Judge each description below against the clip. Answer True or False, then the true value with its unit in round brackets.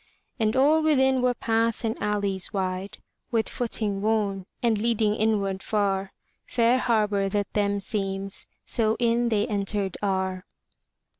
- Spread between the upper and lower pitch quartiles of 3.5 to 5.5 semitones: False (2.8 semitones)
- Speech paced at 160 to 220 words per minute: False (135 wpm)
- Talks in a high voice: True (210 Hz)